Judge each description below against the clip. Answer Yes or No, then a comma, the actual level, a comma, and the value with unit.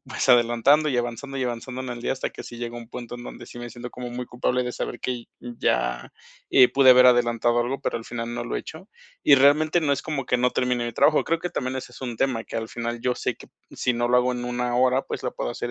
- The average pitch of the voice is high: No, low, 125 Hz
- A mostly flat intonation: Yes, narrow, 1.5 semitones